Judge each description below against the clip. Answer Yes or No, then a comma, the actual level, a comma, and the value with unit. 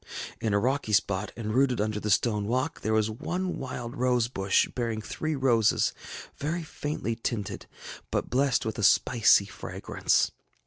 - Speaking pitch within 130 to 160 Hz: No, low, 115 Hz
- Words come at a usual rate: Yes, average, 155 wpm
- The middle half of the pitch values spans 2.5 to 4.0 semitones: Yes, average, 3.7 semitones